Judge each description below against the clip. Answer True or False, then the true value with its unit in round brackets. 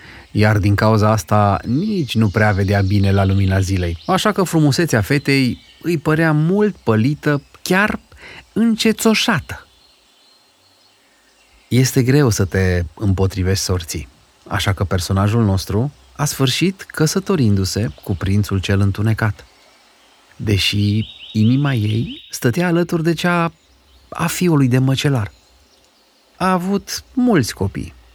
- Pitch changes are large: True (8.5 semitones)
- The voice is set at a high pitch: False (110 Hz)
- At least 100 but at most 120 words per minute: True (115 wpm)